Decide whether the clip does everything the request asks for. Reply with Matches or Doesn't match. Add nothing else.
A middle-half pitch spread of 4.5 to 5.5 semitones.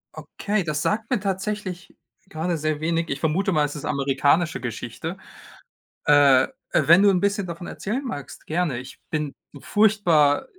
Matches